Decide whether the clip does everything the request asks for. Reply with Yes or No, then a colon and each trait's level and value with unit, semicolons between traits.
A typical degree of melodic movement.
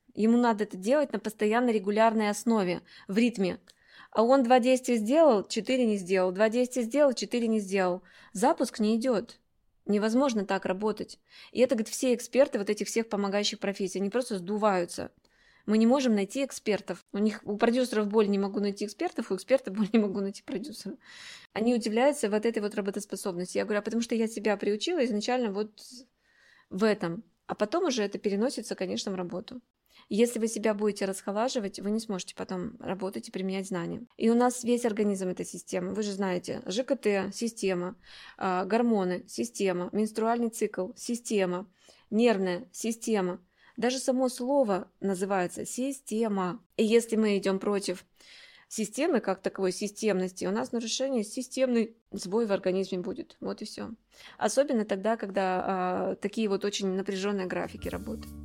Yes: average, 3.4 semitones